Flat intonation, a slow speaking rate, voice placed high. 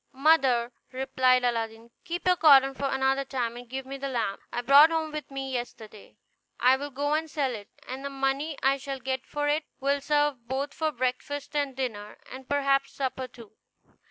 No: narrow, 2.2 semitones; average, 190 wpm; very high, 270 Hz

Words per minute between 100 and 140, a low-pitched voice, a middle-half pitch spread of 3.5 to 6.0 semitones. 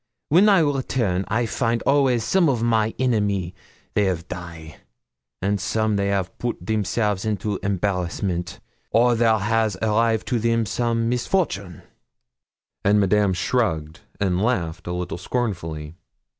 Yes: slow, 135 wpm; low, 105 Hz; average, 4.2 semitones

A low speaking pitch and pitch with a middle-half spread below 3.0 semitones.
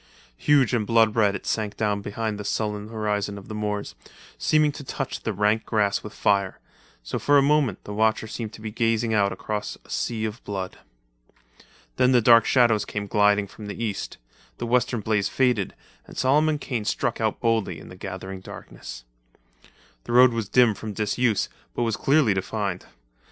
Yes: low, 110 Hz; narrow, 2.5 semitones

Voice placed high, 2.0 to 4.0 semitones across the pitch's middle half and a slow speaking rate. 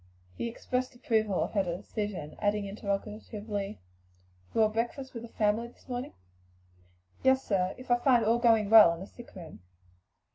No: high, 220 Hz; average, 3.1 semitones; average, 160 wpm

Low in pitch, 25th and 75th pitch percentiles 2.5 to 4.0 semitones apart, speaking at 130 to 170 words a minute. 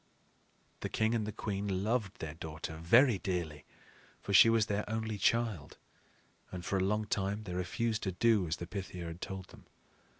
No: low, 100 Hz; average, 3.6 semitones; average, 180 wpm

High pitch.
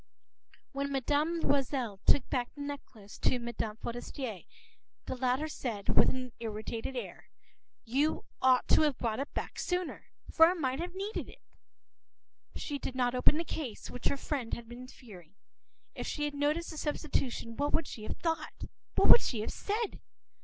Yes: very high, 265 Hz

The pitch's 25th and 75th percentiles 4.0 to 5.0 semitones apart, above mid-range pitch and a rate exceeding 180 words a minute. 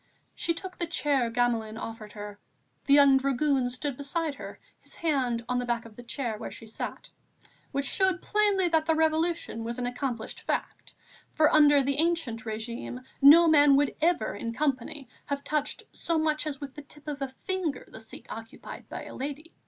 Yes: average, 4.6 semitones; very high, 280 Hz; average, 190 wpm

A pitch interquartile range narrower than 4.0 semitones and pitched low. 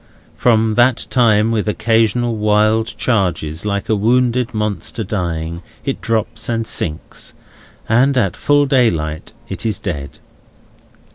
Yes: average, 3.4 semitones; low, 110 Hz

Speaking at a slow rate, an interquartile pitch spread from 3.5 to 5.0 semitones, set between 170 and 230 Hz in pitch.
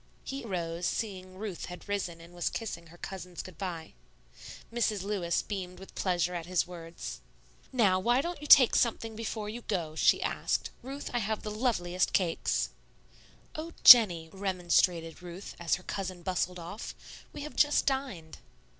No: average, 160 wpm; average, 4.3 semitones; medium, 185 Hz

